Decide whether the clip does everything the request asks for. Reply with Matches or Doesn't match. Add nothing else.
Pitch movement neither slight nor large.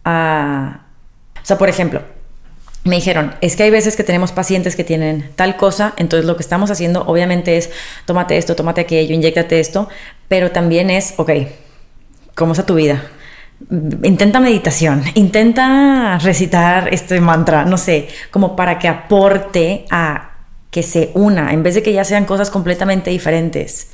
Matches